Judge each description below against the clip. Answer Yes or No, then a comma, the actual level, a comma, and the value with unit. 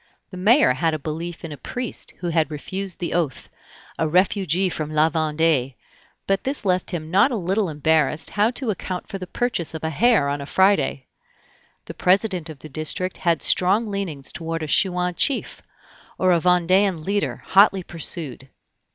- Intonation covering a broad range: No, average, 3.8 semitones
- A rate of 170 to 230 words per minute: Yes, average, 175 wpm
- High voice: No, medium, 175 Hz